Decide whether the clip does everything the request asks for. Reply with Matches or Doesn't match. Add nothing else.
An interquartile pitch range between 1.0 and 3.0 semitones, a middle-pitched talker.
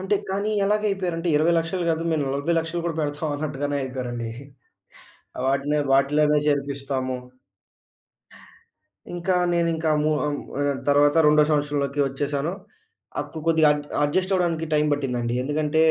Matches